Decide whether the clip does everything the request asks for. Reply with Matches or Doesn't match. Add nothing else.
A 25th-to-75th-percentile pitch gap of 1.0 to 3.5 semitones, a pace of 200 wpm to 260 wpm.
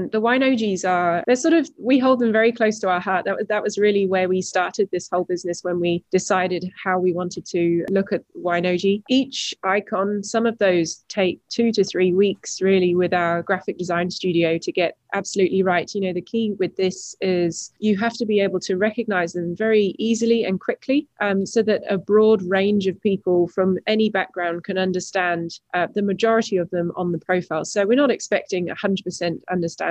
Matches